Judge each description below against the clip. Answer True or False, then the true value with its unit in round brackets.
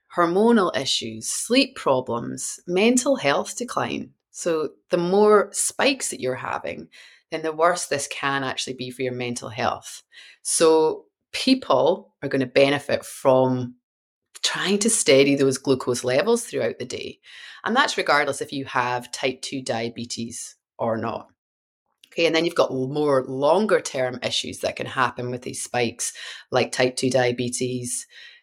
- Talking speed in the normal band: True (150 wpm)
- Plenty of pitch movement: True (6.0 semitones)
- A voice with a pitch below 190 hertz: True (135 Hz)